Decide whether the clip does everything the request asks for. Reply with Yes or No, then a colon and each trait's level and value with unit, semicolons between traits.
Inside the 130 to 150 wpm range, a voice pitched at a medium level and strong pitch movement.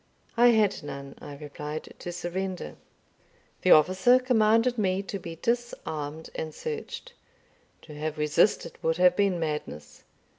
Yes: slow, 135 wpm; medium, 175 Hz; wide, 6.2 semitones